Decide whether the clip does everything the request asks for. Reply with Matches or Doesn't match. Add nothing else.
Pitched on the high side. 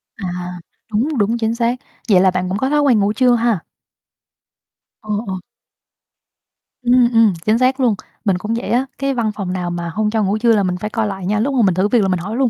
Matches